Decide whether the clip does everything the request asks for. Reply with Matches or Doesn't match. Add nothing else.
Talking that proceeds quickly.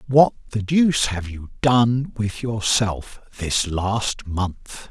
Doesn't match